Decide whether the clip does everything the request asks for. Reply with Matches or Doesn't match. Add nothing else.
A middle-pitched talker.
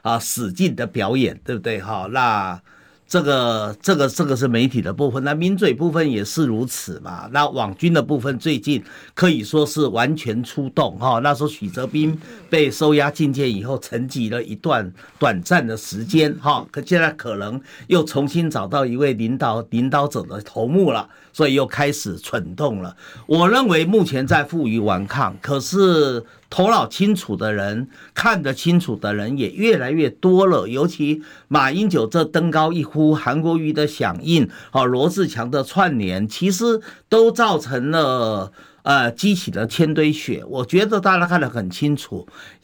Matches